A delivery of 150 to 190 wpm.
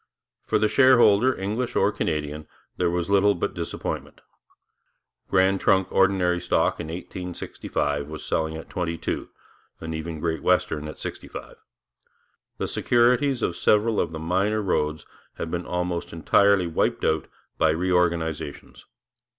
No: slow, 135 wpm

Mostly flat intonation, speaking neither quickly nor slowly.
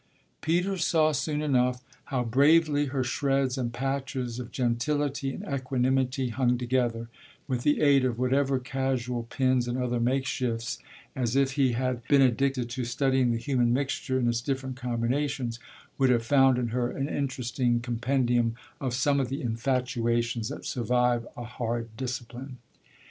Yes: narrow, 2.1 semitones; average, 155 wpm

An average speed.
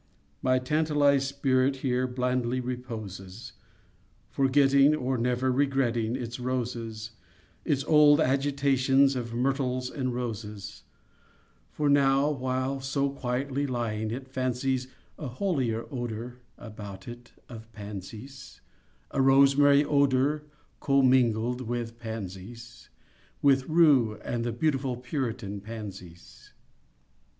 No: slow, 105 wpm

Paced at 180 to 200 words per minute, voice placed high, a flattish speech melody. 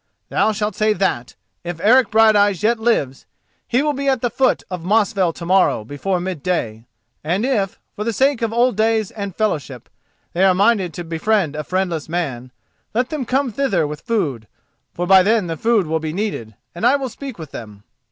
No: average, 190 wpm; high, 195 Hz; wide, 5.6 semitones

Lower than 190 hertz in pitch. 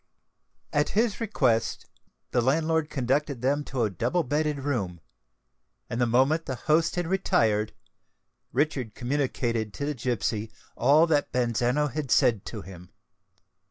Yes: low, 135 Hz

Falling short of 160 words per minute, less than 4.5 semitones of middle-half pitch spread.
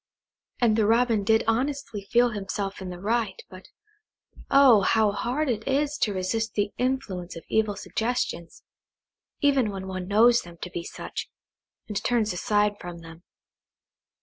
Yes: average, 150 wpm; average, 4.1 semitones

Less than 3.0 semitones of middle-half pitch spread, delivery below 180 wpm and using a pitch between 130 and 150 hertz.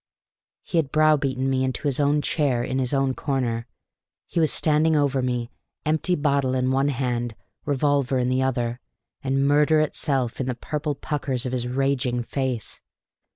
Yes: narrow, 2.4 semitones; average, 165 wpm; low, 135 Hz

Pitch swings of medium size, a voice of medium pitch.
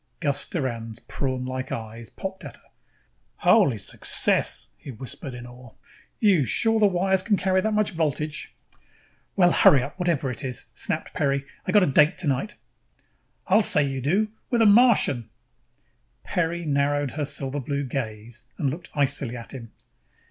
No: wide, 6.3 semitones; medium, 145 Hz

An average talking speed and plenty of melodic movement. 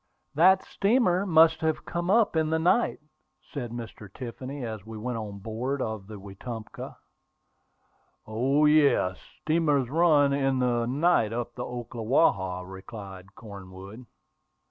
No: slow, 130 wpm; wide, 6.3 semitones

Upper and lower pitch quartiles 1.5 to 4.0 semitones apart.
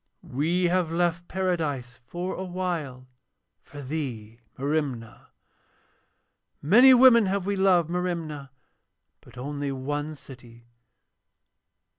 No: average, 4.9 semitones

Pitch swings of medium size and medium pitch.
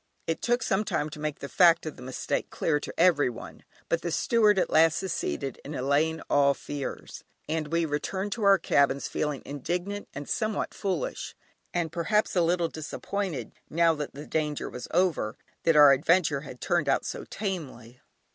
Yes: average, 4.0 semitones; medium, 160 Hz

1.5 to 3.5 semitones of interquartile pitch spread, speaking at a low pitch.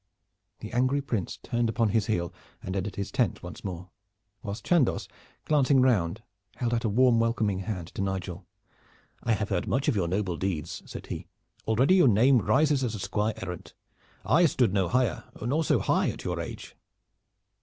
No: average, 4.8 semitones; low, 110 Hz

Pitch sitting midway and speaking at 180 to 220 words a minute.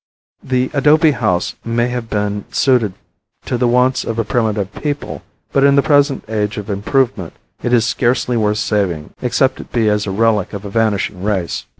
No: low, 115 Hz; average, 185 wpm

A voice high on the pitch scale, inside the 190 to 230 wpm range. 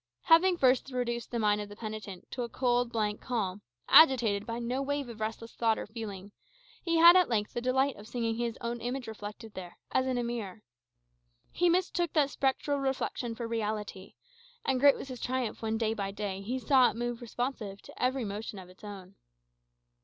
Yes: high, 235 Hz; average, 200 wpm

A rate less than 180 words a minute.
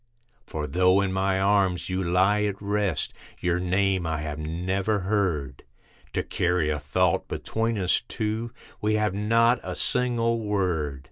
Yes: average, 150 wpm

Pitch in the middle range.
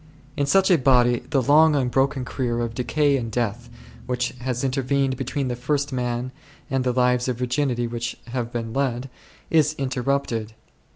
No: low, 125 Hz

